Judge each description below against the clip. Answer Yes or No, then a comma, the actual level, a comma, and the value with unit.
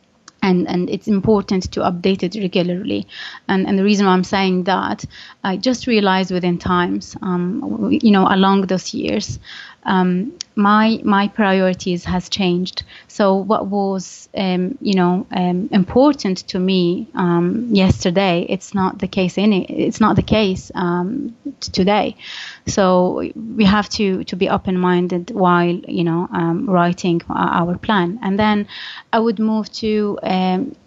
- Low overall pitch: No, high, 190 Hz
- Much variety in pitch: No, narrow, 2.6 semitones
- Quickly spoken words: No, average, 155 wpm